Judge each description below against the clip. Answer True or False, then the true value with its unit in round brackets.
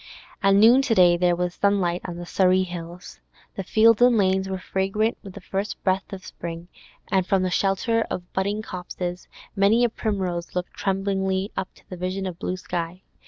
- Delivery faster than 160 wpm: True (190 wpm)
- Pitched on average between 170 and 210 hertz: True (190 Hz)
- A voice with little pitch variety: True (2.0 semitones)